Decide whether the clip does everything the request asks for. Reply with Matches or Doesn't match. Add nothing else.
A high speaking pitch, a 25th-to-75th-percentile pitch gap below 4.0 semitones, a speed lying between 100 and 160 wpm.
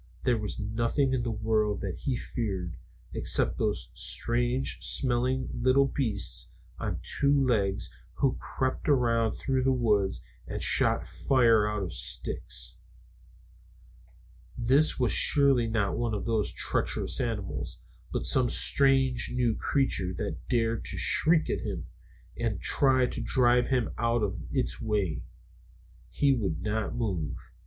Doesn't match